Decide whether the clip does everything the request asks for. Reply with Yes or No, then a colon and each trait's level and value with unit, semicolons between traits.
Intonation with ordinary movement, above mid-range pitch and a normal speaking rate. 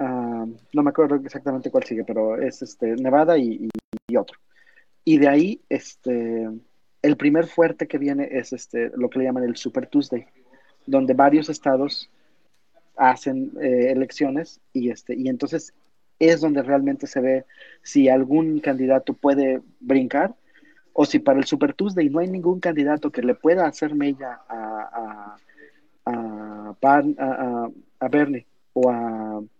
No: average, 3.6 semitones; low, 135 Hz; average, 160 wpm